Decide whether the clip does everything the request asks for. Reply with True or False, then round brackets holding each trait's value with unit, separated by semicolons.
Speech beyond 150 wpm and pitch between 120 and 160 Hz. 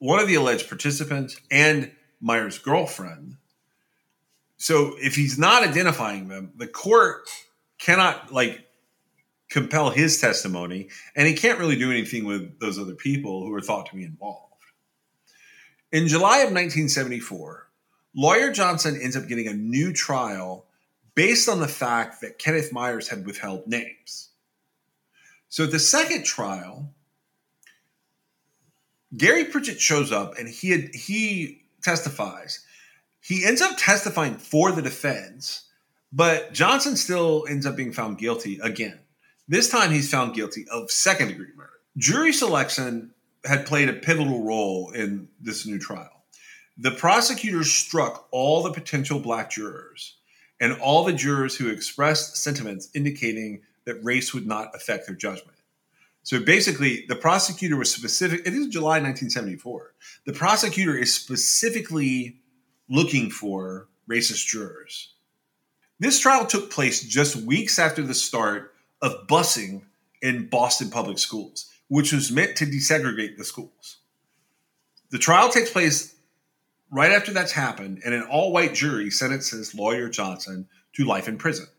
False (140 wpm; 140 Hz)